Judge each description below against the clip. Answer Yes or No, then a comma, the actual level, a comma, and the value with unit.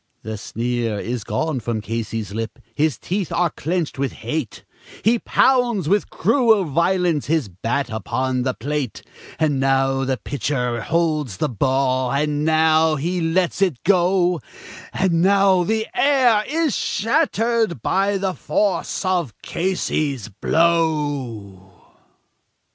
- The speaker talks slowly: Yes, slow, 125 wpm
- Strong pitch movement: Yes, wide, 6.6 semitones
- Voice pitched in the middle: Yes, medium, 155 Hz